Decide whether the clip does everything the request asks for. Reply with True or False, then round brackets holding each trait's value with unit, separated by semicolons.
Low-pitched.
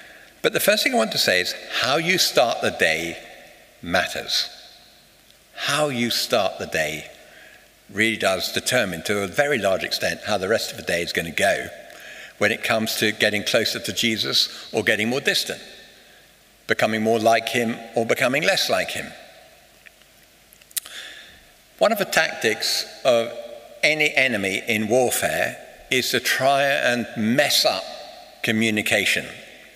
True (115 Hz)